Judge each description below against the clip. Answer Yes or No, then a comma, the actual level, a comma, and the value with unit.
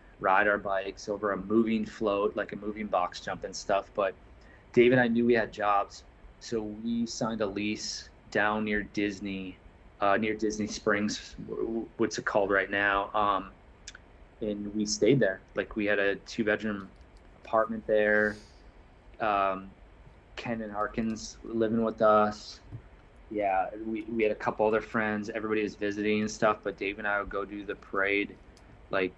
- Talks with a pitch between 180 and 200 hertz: No, low, 105 Hz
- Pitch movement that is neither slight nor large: No, narrow, 1.8 semitones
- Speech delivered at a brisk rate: No, average, 170 wpm